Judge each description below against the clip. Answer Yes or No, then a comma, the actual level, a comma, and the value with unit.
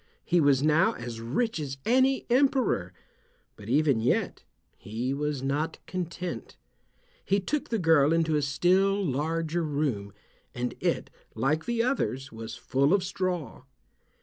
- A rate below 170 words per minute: Yes, average, 140 wpm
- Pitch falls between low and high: Yes, medium, 155 Hz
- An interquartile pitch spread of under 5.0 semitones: No, wide, 5.5 semitones